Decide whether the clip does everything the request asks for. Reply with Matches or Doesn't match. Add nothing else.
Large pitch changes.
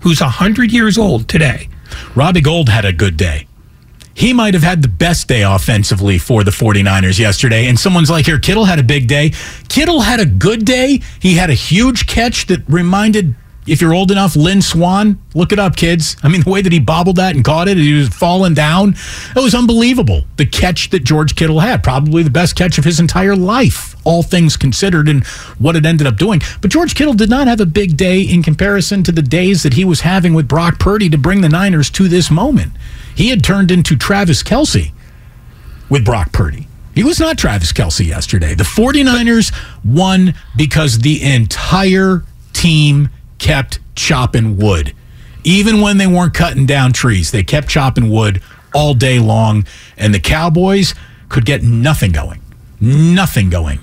Matches